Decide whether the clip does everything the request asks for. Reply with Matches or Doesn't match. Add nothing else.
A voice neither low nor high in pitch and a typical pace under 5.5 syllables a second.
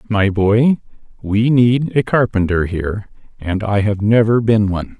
Doesn't match